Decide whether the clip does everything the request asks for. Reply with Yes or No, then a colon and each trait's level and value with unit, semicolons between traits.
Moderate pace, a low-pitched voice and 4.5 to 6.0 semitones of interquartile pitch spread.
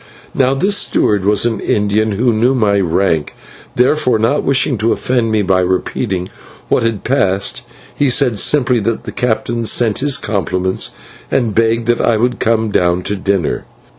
No: average, 165 wpm; low, 110 Hz; average, 3.8 semitones